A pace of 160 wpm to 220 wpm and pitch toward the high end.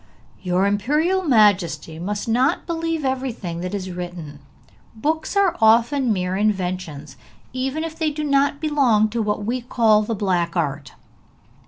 No: average, 145 wpm; high, 215 Hz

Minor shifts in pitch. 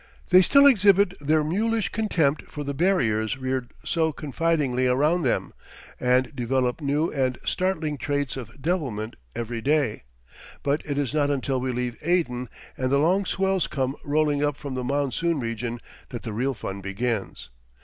No: average, 4.3 semitones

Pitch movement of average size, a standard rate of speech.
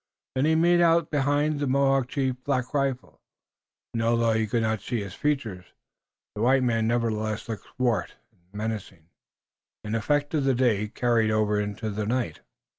Yes: average, 4.1 semitones; average, 170 wpm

